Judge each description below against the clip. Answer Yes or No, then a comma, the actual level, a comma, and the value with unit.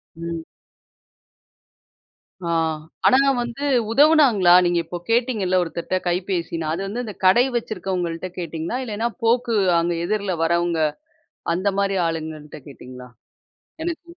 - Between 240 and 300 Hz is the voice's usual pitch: No, medium, 185 Hz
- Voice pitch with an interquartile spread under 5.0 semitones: No, wide, 5.4 semitones